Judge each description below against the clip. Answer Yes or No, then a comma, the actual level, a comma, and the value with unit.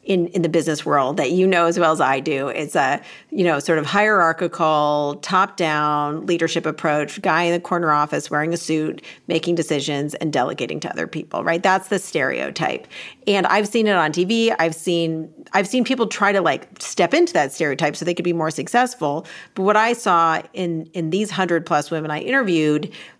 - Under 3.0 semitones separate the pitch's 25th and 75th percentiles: No, average, 3.5 semitones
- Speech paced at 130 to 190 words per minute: No, fast, 205 wpm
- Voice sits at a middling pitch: Yes, medium, 170 Hz